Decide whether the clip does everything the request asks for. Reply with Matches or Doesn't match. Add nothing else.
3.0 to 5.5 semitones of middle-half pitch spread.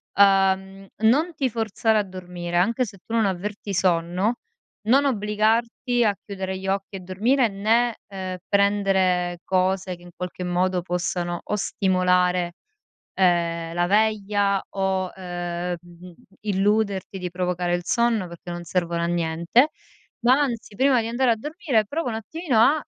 Matches